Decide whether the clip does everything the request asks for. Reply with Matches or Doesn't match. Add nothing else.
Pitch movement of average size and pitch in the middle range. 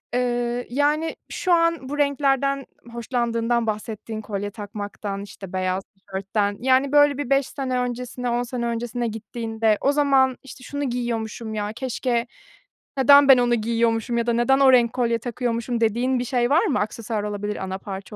Doesn't match